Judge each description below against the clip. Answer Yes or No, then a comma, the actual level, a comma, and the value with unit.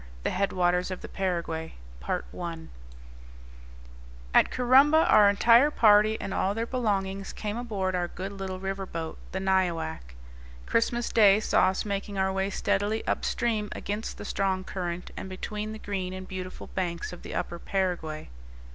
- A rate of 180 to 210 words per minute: No, average, 155 wpm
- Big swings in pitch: No, narrow, 2.4 semitones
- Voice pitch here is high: Yes, high, 195 Hz